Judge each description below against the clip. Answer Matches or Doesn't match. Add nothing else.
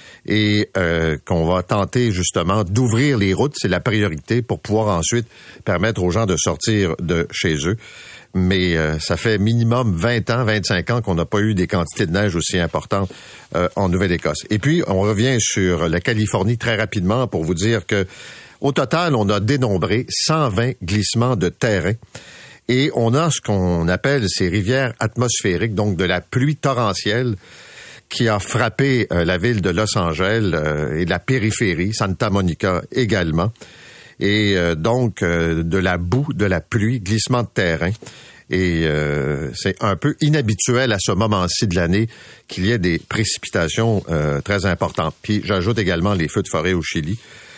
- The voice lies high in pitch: Doesn't match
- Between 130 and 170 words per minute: Matches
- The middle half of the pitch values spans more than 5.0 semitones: Doesn't match